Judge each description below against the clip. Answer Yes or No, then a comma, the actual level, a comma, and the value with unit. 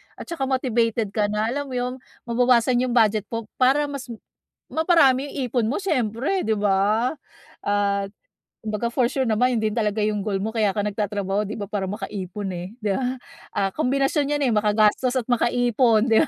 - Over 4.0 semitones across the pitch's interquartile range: No, average, 3.5 semitones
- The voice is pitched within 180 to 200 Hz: No, high, 225 Hz